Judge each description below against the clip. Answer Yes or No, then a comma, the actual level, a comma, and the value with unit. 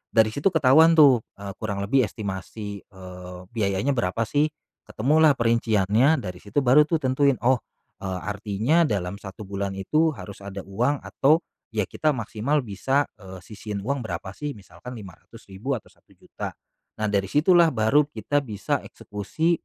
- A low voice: Yes, low, 110 Hz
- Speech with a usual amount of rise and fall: No, wide, 6.3 semitones